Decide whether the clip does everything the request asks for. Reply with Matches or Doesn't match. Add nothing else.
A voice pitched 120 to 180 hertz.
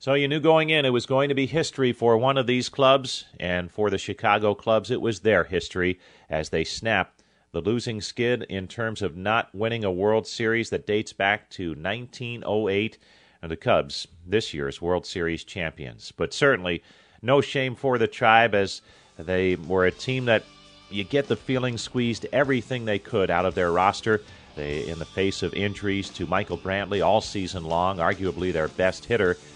Doesn't match